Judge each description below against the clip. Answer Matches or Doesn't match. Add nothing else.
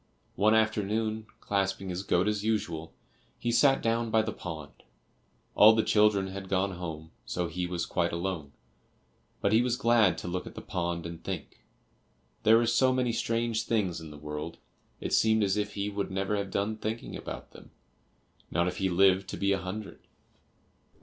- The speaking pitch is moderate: Doesn't match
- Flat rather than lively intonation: Doesn't match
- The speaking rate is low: Doesn't match